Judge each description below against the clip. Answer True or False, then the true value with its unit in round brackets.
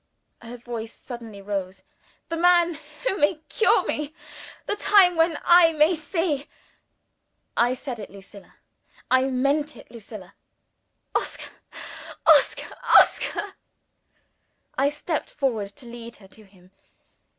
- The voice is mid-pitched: False (270 Hz)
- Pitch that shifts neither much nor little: False (6.6 semitones)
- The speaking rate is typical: False (120 wpm)